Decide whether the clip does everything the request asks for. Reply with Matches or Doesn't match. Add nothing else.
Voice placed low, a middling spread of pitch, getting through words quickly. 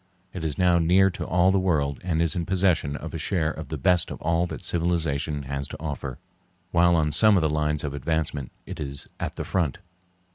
Matches